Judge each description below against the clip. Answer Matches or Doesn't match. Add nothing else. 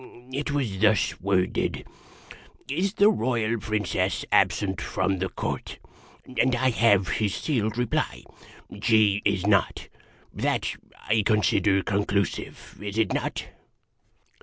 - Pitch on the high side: Doesn't match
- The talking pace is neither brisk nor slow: Doesn't match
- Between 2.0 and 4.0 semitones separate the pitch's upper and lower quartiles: Matches